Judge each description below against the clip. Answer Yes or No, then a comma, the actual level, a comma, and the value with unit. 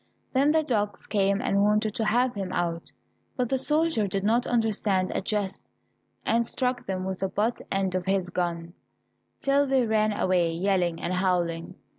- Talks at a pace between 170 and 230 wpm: Yes, average, 175 wpm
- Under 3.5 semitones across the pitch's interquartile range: No, average, 4.2 semitones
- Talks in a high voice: Yes, high, 200 Hz